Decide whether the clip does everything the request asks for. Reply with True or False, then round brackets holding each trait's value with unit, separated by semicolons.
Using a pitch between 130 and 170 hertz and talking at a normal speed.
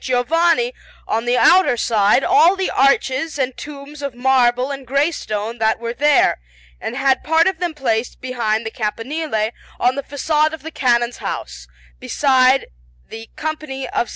False (265 Hz; 165 wpm)